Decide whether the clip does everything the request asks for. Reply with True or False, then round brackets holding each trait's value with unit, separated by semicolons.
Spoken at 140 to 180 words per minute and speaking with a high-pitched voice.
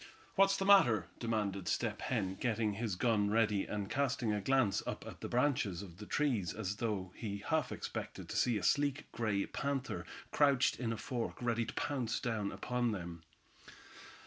False (175 wpm; 115 Hz)